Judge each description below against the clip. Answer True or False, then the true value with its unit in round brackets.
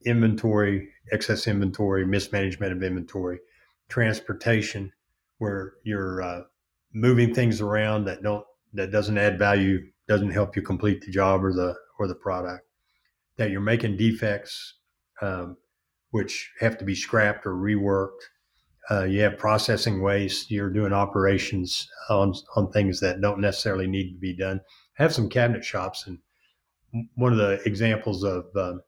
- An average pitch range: False (2.0 semitones)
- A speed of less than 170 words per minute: True (150 wpm)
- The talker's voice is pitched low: True (100 Hz)